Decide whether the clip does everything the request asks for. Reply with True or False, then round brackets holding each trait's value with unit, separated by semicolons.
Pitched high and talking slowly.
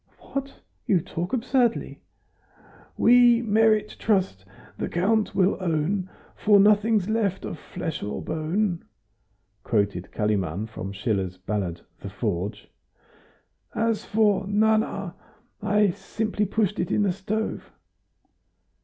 True (195 Hz; 110 wpm)